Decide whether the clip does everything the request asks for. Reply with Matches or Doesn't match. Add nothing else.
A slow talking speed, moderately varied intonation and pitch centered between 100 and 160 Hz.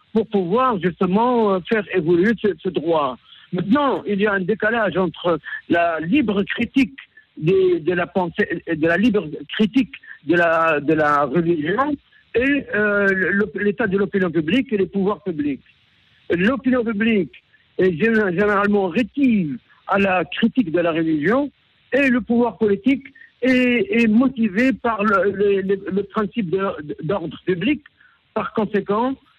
Doesn't match